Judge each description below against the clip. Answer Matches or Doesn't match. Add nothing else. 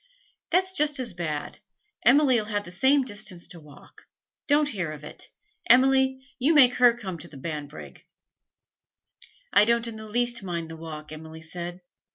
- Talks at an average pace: Matches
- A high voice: Matches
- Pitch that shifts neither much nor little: Doesn't match